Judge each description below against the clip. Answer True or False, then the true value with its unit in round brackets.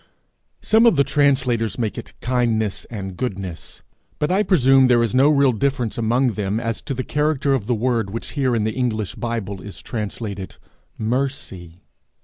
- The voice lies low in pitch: True (120 Hz)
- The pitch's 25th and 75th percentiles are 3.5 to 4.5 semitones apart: True (4.0 semitones)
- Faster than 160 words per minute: True (170 wpm)